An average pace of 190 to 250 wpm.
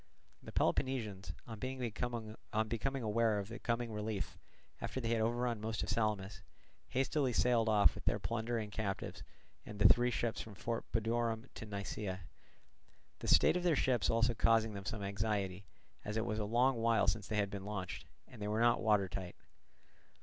No: average, 180 wpm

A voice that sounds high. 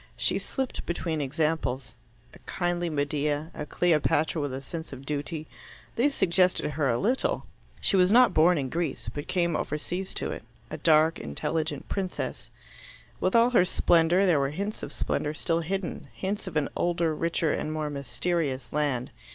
No: medium, 160 Hz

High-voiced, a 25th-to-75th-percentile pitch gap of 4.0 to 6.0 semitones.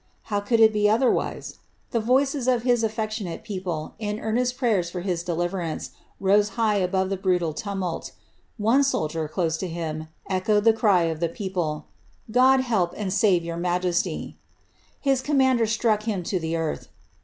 Yes: high, 200 Hz; average, 4.5 semitones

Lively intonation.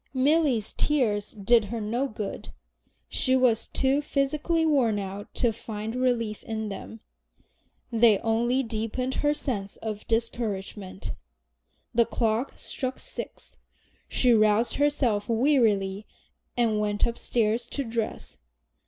No: average, 3.3 semitones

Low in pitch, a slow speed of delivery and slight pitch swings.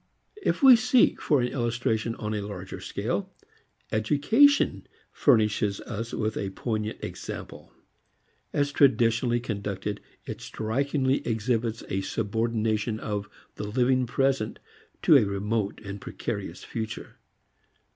No: low, 115 Hz; slow, 115 wpm; average, 3.5 semitones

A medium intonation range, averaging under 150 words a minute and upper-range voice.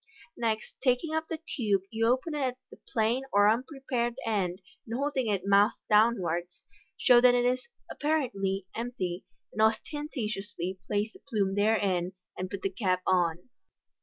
No: average, 4.5 semitones; average, 155 wpm; high, 220 Hz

